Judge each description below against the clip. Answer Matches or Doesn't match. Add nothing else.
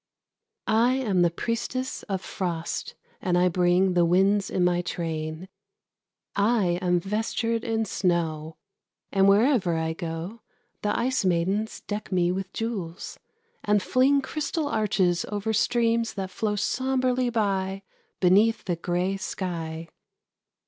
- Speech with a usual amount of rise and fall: Matches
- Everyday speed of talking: Doesn't match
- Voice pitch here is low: Doesn't match